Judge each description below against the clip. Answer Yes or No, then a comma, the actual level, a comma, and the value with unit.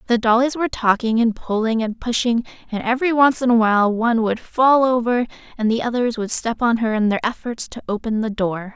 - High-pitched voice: Yes, high, 230 Hz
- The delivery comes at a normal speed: No, fast, 220 wpm